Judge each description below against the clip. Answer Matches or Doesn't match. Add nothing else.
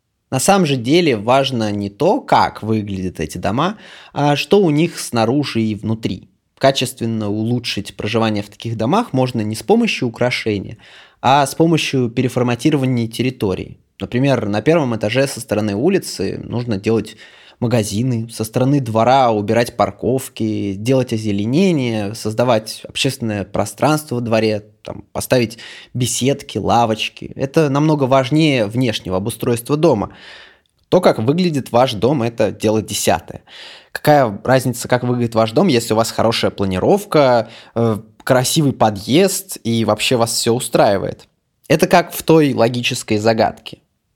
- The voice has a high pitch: Doesn't match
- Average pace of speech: Matches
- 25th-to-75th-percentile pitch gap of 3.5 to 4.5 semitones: Matches